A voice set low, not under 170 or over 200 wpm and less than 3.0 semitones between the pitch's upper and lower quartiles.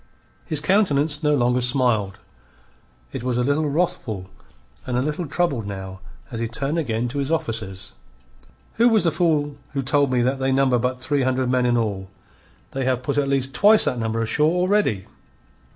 No: low, 130 Hz; average, 185 wpm; average, 3.9 semitones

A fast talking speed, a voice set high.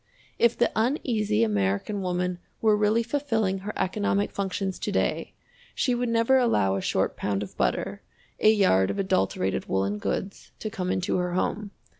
No: average, 165 wpm; high, 195 Hz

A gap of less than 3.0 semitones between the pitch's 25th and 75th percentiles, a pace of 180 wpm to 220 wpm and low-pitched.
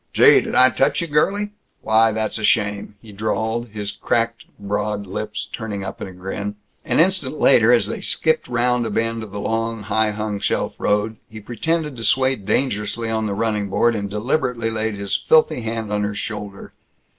Yes: narrow, 2.4 semitones; average, 190 wpm; low, 110 Hz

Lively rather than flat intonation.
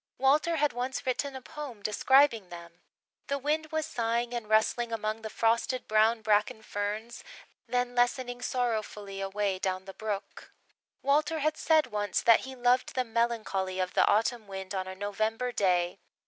No: average, 3.8 semitones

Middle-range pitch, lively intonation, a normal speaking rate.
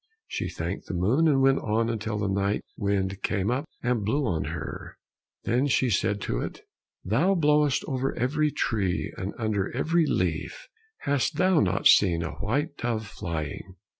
No: low, 115 Hz; wide, 6.2 semitones; average, 165 wpm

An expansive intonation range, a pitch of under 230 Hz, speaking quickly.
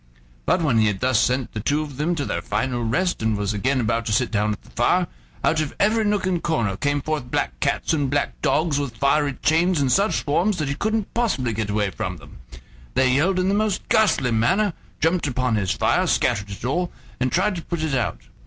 Yes: wide, 7.2 semitones; medium, 140 Hz; fast, 230 wpm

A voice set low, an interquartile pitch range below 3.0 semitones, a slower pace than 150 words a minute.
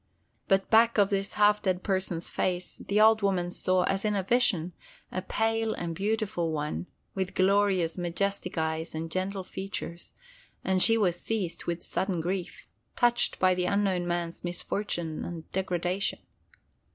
No: medium, 185 Hz; narrow, 2.6 semitones; average, 140 wpm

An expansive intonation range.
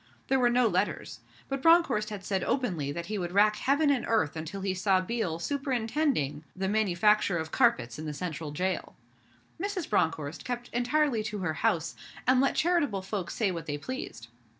Yes: wide, 6.8 semitones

